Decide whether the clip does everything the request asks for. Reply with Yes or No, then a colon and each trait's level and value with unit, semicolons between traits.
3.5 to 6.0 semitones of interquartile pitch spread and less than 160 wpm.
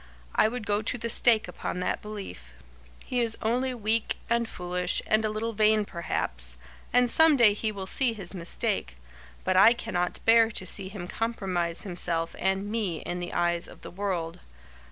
No: average, 4.3 semitones; average, 180 wpm